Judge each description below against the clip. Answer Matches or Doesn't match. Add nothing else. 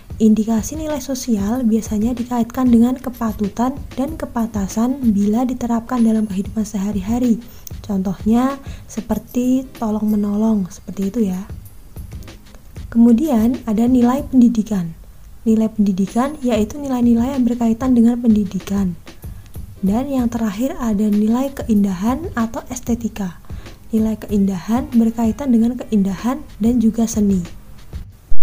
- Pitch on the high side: Matches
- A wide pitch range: Doesn't match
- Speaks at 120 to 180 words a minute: Doesn't match